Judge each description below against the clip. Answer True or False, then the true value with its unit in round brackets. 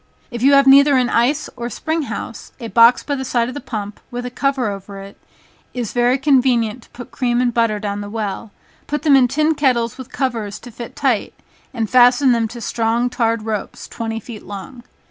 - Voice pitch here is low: False (240 Hz)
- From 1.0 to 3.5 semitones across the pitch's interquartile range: True (2.8 semitones)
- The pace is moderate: False (210 wpm)